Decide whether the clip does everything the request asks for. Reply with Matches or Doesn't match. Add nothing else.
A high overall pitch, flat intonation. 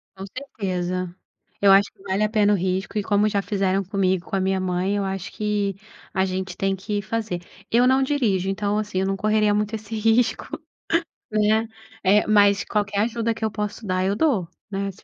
Matches